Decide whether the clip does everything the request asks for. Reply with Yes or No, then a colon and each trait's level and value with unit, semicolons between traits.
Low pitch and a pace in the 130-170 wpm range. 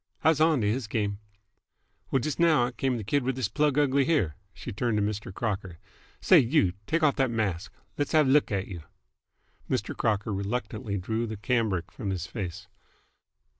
No: low, 115 Hz; average, 190 wpm